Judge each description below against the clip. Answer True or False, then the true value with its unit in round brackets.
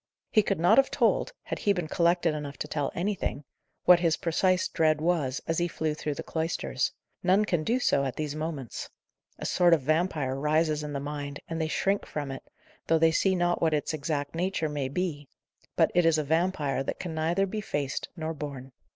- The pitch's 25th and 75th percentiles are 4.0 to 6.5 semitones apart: False (3.0 semitones)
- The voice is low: False (160 Hz)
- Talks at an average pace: False (210 wpm)